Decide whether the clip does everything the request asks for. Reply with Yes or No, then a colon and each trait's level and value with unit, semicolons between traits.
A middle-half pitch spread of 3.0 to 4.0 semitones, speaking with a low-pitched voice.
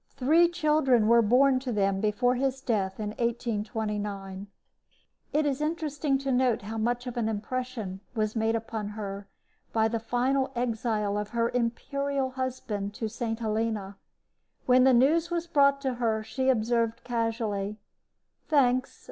No: average, 3.4 semitones; high, 235 Hz